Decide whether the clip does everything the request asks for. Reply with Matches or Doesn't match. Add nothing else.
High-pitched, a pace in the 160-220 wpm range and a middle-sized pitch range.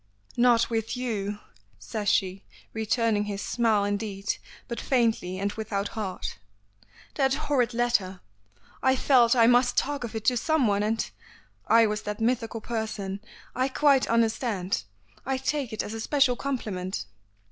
Doesn't match